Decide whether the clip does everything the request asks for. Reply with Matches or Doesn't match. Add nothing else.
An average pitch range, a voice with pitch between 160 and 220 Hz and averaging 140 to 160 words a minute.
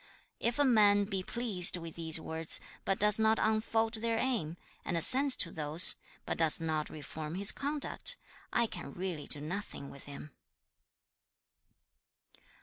Doesn't match